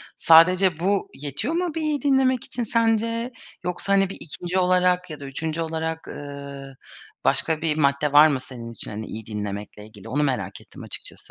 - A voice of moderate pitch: Yes, medium, 160 Hz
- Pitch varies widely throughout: Yes, wide, 5.8 semitones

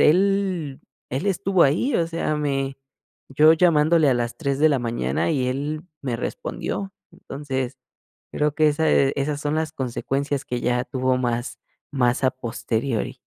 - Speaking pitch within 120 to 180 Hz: Yes, medium, 140 Hz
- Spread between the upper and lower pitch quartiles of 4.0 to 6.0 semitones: No, average, 3.5 semitones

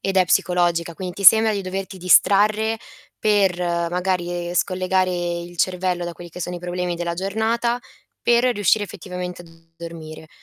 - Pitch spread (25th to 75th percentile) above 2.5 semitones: No, narrow, 2.2 semitones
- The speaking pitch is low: No, medium, 180 Hz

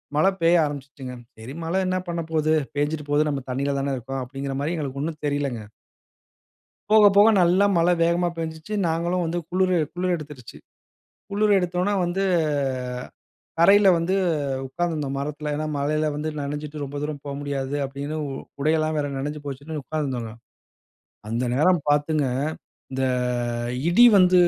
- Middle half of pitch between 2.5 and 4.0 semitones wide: Yes, average, 3.6 semitones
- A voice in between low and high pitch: Yes, medium, 150 Hz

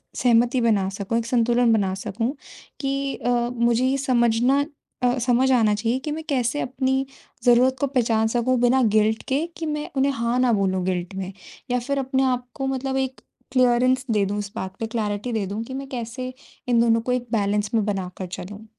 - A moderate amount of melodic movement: Yes, average, 3.3 semitones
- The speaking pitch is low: No, high, 240 Hz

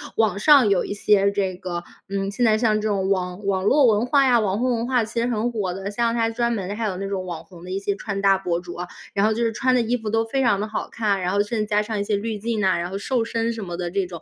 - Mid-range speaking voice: No, high, 210 Hz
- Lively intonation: No, average, 2.9 semitones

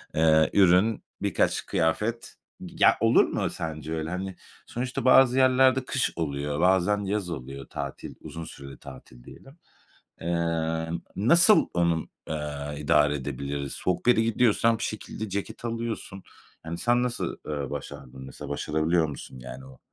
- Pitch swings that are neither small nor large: No, wide, 7.3 semitones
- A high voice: No, very low, 85 Hz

